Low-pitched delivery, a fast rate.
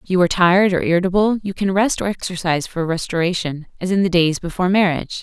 No: medium, 180 Hz; fast, 220 wpm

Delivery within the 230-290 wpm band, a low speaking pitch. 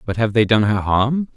Yes: fast, 265 wpm; low, 115 Hz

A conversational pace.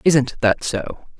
Yes: average, 150 wpm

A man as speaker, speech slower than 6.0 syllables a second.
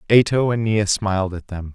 No: male; 6.6 syllables/s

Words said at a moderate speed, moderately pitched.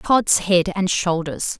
Yes: average, 150 wpm; medium, 180 Hz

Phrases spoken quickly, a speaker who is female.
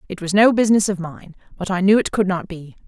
Yes: fast, 270 wpm; female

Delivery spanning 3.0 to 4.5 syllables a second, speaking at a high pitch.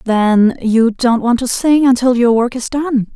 Yes: 4.1 syllables/s; high, 240 Hz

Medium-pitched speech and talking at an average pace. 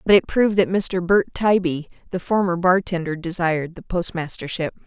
Yes: medium, 180 Hz; average, 160 wpm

